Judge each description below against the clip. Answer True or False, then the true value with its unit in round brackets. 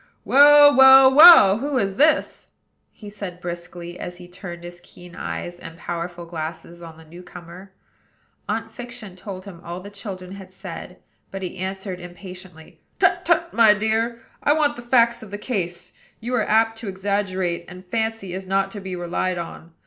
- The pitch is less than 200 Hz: True (190 Hz)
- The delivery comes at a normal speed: True (180 wpm)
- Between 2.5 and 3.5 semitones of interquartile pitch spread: False (4.2 semitones)